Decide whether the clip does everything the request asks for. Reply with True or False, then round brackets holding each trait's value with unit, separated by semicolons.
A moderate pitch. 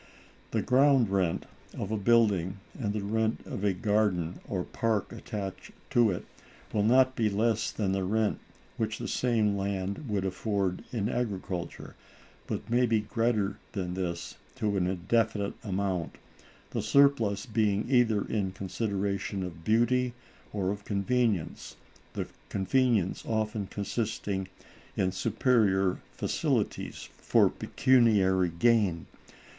False (105 Hz)